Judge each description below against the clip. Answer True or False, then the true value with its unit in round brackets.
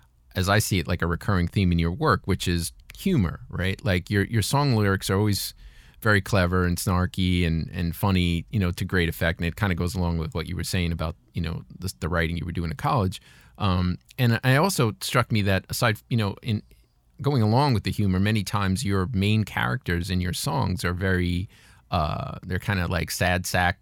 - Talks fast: True (225 wpm)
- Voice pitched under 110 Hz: True (95 Hz)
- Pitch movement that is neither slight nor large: True (3.3 semitones)